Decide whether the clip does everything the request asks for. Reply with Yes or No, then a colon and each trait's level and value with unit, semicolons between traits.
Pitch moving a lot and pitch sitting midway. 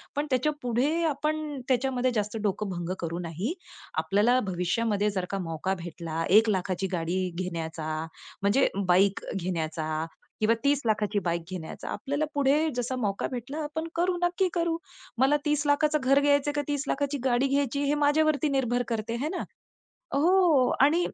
No: wide, 7.2 semitones; very high, 250 Hz